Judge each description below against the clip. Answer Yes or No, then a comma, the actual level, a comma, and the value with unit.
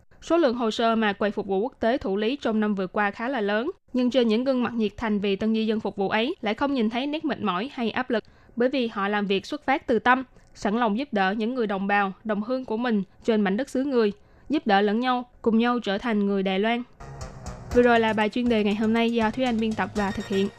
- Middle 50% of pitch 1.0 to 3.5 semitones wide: Yes, average, 2.9 semitones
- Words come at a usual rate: No, fast, 285 wpm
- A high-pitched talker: Yes, high, 220 Hz